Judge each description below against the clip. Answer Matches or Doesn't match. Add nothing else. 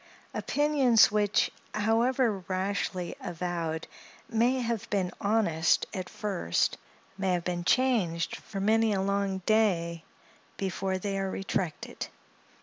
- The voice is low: Doesn't match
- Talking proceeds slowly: Matches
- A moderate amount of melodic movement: Matches